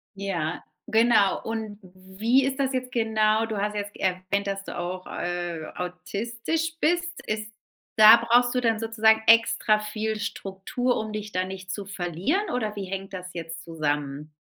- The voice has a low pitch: No, high, 210 Hz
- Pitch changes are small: No, average, 3.6 semitones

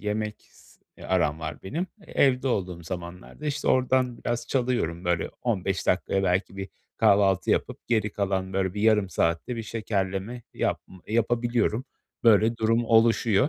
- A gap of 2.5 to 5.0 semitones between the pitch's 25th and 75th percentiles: Yes, average, 4.0 semitones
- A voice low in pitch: Yes, low, 105 Hz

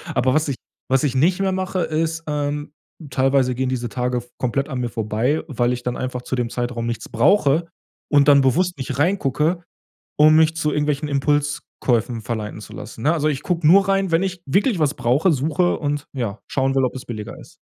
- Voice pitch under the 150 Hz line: Yes, medium, 140 Hz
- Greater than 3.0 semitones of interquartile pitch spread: Yes, average, 4.2 semitones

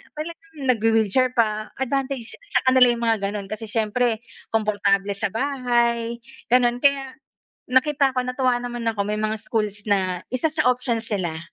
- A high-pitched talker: Yes, high, 235 Hz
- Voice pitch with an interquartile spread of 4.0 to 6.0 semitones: No, average, 3.1 semitones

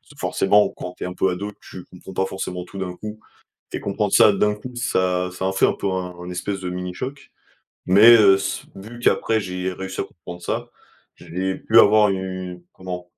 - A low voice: Yes, very low, 95 Hz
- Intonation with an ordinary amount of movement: No, narrow, 2.2 semitones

